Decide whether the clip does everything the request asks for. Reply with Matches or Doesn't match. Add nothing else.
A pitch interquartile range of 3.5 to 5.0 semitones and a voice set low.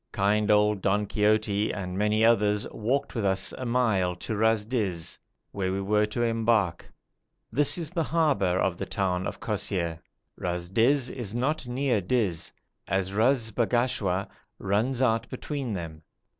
Matches